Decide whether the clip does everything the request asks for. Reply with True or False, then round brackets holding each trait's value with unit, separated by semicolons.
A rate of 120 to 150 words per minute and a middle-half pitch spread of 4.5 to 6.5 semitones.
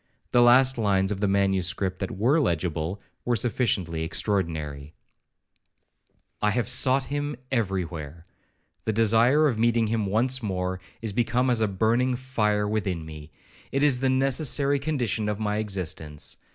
True (140 wpm; 5.0 semitones)